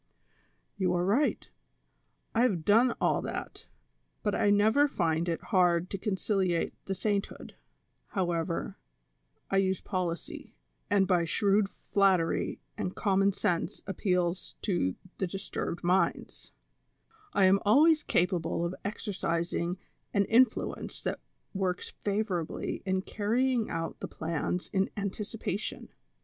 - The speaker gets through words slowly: Yes, slow, 125 wpm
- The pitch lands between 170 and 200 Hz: Yes, high, 190 Hz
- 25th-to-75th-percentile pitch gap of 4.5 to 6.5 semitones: No, average, 2.9 semitones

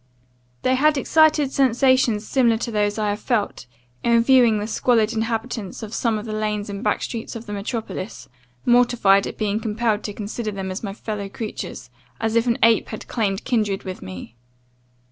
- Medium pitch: No, high, 220 Hz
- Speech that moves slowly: No, average, 185 wpm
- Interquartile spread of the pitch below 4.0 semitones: Yes, narrow, 2.5 semitones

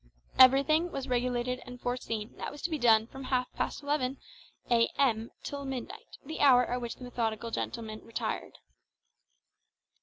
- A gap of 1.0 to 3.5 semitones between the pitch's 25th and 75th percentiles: Yes, narrow, 2.6 semitones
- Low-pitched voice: No, very high, 250 Hz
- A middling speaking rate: Yes, average, 150 wpm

